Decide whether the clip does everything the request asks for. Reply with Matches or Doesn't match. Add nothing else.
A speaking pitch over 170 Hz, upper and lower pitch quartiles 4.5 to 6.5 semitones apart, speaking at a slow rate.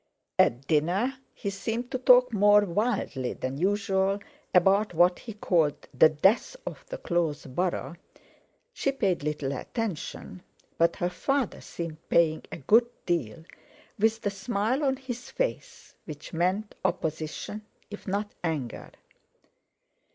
Matches